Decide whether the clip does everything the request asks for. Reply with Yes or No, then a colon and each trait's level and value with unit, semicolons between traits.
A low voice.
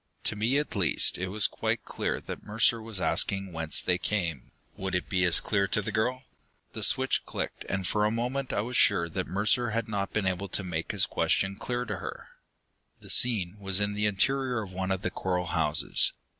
Yes: low, 100 Hz